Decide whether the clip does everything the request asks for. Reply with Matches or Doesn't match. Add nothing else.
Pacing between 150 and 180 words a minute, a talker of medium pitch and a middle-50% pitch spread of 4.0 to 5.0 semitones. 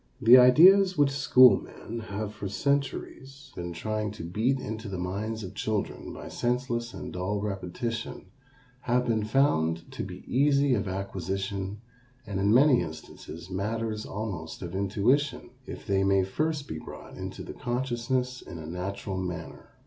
Doesn't match